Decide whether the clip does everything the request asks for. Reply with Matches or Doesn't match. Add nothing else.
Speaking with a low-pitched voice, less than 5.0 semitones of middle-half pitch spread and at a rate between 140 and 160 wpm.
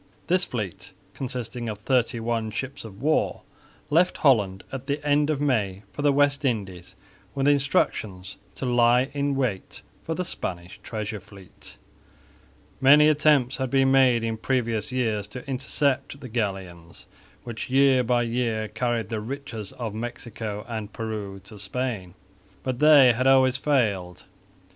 Matches